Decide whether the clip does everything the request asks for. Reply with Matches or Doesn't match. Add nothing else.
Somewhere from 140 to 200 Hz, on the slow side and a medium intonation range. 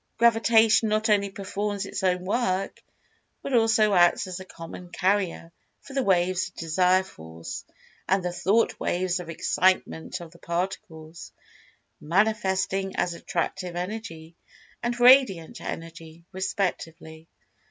Matches